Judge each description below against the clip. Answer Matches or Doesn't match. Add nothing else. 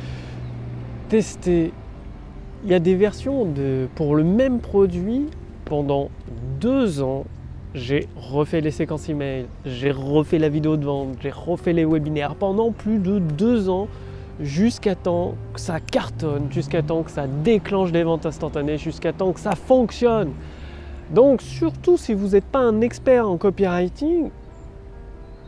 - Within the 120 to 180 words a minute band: Matches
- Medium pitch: Matches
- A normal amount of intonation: Doesn't match